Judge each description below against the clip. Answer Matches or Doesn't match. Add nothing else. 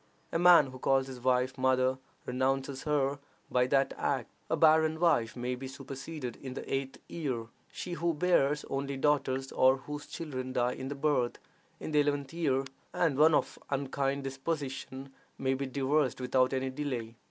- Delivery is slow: Doesn't match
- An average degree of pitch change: Doesn't match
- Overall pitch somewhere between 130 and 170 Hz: Matches